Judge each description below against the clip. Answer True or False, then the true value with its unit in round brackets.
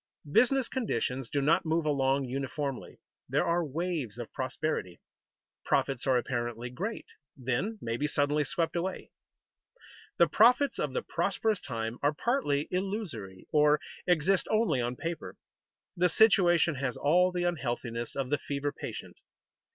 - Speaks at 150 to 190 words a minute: False (140 wpm)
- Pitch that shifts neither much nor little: False (5.7 semitones)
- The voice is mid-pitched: True (150 Hz)